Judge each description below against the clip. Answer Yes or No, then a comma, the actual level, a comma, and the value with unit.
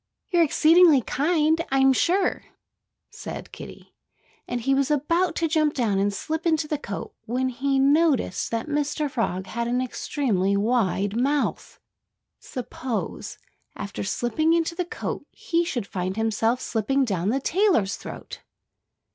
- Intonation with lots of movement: Yes, wide, 5.8 semitones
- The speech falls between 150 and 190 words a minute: No, average, 140 wpm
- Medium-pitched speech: No, very high, 270 Hz